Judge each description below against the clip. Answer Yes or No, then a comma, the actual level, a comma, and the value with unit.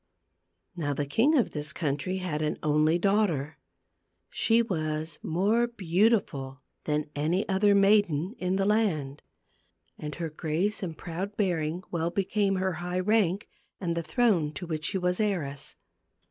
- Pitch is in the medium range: Yes, medium, 175 Hz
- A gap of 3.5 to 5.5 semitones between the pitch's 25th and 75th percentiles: Yes, average, 4.5 semitones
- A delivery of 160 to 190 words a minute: No, average, 145 wpm